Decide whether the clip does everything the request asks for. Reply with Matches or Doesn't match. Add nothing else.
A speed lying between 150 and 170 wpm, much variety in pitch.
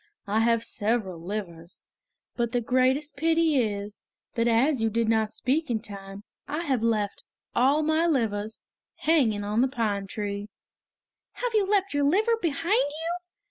Matches